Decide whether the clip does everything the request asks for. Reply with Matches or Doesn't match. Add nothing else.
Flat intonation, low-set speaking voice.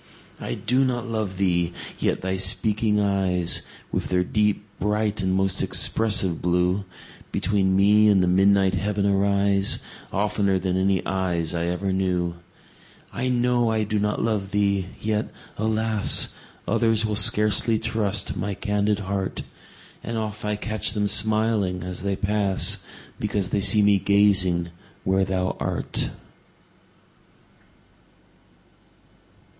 Matches